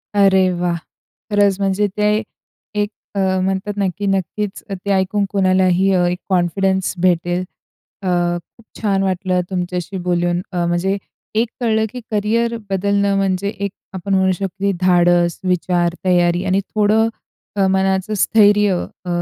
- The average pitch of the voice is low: No, high, 190 Hz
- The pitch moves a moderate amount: No, narrow, 1.9 semitones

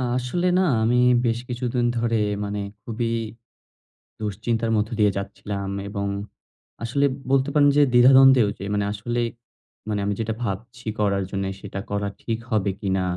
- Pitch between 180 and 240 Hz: No, low, 110 Hz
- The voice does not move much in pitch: No, average, 3.2 semitones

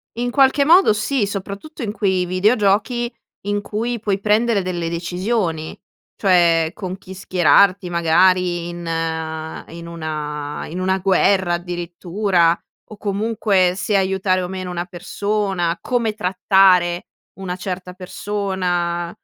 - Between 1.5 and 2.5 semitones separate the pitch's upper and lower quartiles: No, average, 2.9 semitones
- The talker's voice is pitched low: No, medium, 185 Hz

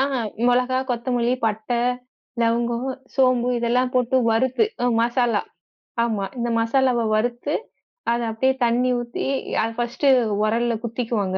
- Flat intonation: Yes, narrow, 1.6 semitones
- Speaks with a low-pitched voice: No, high, 240 Hz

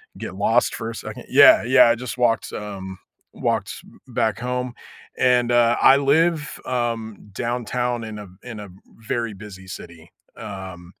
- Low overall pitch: Yes, low, 115 Hz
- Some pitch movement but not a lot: Yes, average, 3.3 semitones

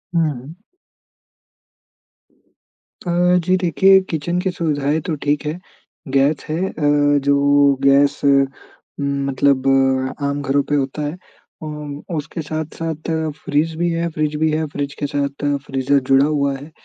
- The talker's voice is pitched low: No, medium, 145 Hz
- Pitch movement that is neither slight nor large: No, narrow, 2.1 semitones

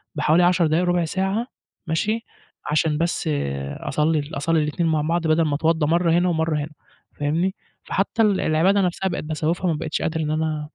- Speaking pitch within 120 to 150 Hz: No, medium, 165 Hz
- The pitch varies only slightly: Yes, narrow, 2.3 semitones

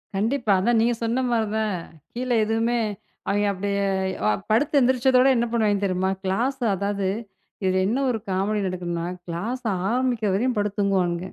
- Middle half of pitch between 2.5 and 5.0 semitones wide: Yes, average, 3.8 semitones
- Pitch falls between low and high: No, high, 215 Hz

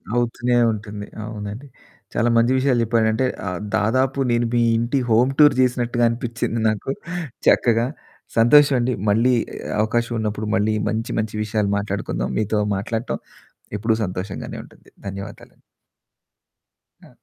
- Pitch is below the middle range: Yes, low, 115 Hz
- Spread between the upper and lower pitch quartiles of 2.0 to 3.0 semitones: Yes, narrow, 2.4 semitones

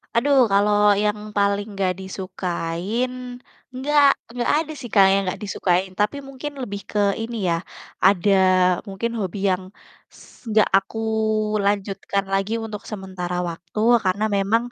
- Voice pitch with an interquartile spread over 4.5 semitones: No, average, 2.9 semitones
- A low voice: No, high, 200 Hz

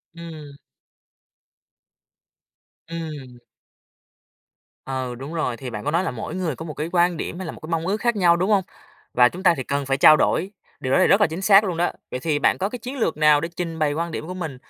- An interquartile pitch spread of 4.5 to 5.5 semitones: No, average, 4.1 semitones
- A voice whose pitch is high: No, medium, 165 Hz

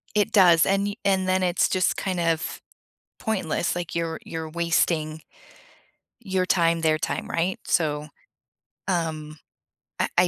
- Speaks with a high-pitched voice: No, medium, 170 Hz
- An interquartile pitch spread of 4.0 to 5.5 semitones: No, narrow, 2.6 semitones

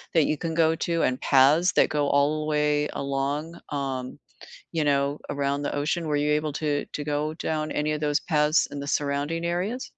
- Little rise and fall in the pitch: Yes, narrow, 1.7 semitones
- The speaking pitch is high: No, medium, 150 Hz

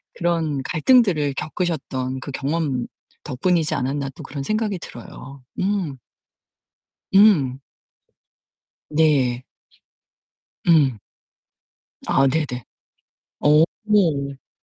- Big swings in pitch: No, average, 4.3 semitones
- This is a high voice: No, medium, 150 Hz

